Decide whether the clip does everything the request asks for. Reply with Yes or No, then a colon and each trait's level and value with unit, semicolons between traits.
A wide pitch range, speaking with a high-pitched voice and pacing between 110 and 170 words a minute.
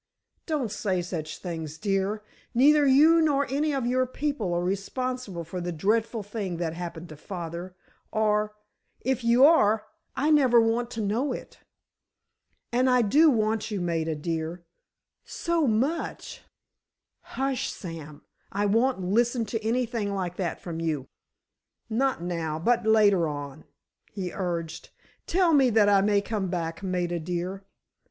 Yes: wide, 6.0 semitones; high, 205 Hz; average, 140 wpm